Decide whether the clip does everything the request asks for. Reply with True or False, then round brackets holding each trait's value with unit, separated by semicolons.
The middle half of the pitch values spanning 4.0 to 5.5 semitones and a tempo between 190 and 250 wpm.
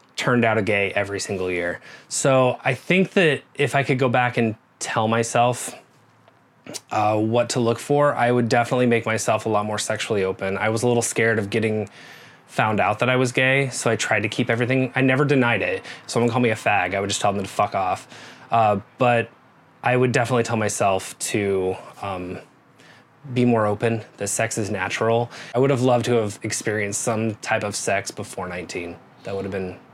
False (2.9 semitones; 205 wpm)